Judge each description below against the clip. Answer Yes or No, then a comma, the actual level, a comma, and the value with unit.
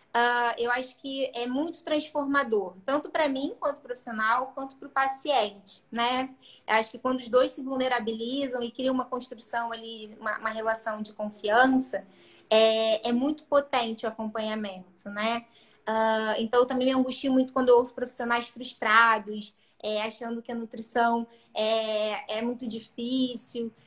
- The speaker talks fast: No, average, 155 wpm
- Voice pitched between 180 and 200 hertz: No, high, 235 Hz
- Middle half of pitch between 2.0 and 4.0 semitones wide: Yes, average, 2.8 semitones